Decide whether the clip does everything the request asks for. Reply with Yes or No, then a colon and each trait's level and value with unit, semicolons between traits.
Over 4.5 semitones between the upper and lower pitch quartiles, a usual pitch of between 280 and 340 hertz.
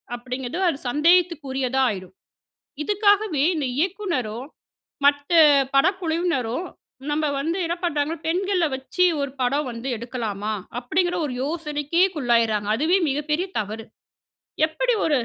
Yes: wide, 5.4 semitones; very high, 295 Hz